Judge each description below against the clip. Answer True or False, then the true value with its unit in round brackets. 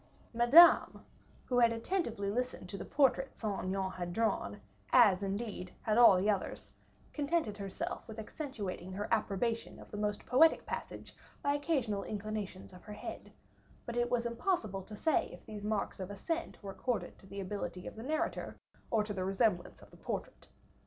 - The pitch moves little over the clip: False (3.7 semitones)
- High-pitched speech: True (215 Hz)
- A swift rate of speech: False (175 wpm)